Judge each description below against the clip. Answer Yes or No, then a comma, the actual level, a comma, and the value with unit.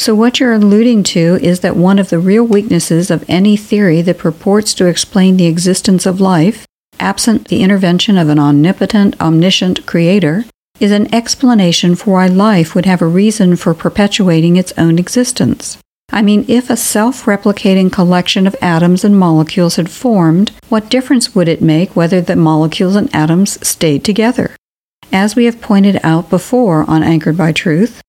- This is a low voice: No, high, 190 Hz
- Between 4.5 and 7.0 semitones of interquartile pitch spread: No, average, 3.7 semitones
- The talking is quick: No, average, 175 wpm